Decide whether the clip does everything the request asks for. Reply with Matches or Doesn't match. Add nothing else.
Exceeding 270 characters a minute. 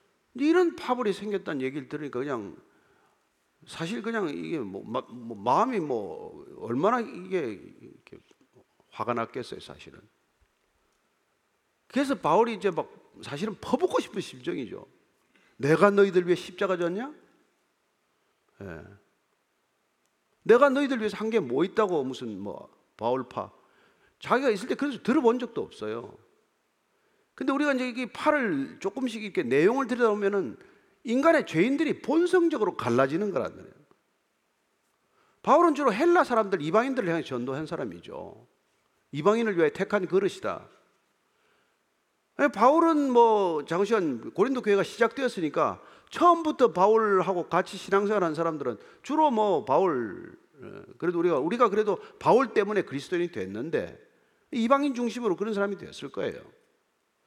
Matches